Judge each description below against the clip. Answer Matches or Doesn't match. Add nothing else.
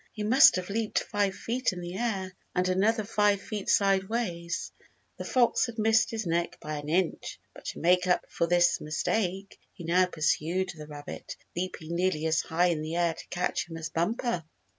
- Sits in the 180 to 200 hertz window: Matches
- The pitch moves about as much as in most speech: Matches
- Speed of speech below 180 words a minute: Doesn't match